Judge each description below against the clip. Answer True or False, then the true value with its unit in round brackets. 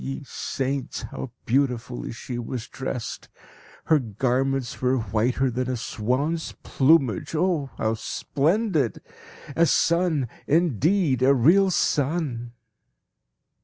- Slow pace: True (105 wpm)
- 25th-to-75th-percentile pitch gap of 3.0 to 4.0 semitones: False (4.6 semitones)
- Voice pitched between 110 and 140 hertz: True (135 Hz)